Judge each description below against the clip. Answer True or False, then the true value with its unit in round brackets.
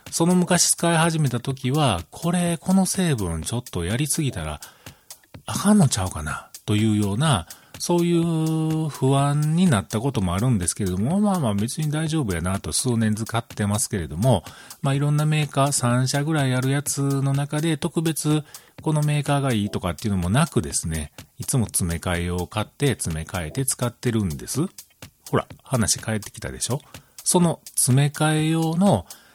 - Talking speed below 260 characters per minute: False (355 characters per minute)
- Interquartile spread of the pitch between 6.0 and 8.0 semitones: True (6.9 semitones)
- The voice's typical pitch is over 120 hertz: True (135 Hz)